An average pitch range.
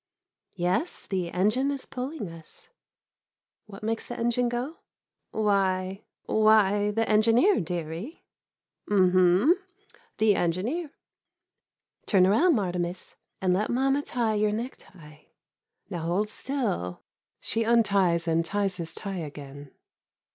Yes: average, 4.7 semitones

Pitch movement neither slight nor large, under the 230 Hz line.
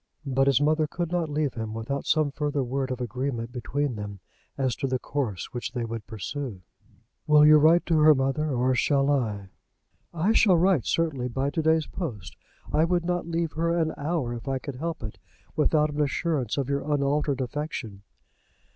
Yes: average, 3.9 semitones; medium, 140 Hz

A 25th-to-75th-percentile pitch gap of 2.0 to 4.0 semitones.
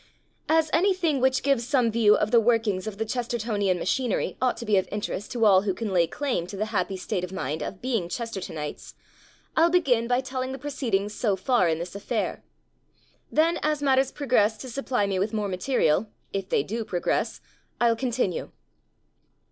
No: average, 4.9 semitones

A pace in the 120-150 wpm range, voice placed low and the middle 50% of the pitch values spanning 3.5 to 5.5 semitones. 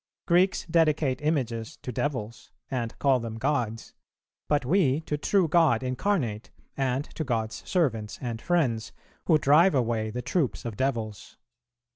Yes: average, 140 wpm; low, 130 Hz; average, 5.2 semitones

